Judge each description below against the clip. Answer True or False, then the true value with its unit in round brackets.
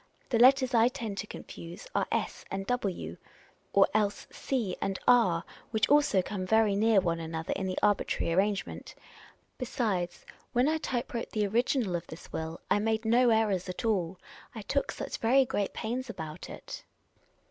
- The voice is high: True (210 Hz)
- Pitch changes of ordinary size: True (4.4 semitones)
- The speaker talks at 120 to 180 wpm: True (170 wpm)